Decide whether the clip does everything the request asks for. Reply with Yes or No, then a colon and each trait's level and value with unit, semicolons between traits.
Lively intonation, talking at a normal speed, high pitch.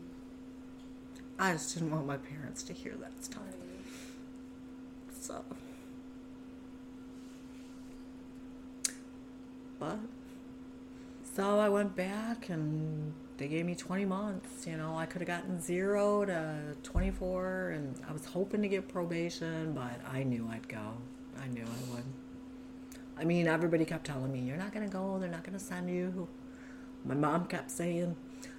Yes: wide, 8.1 semitones; average, 145 wpm; high, 200 Hz